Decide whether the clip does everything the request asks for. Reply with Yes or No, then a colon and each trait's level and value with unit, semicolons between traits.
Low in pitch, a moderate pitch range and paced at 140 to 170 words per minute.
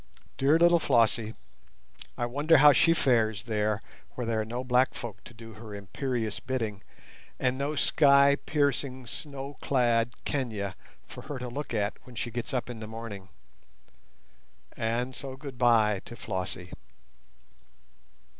Yes: low, 120 Hz; average, 3.7 semitones; average, 145 wpm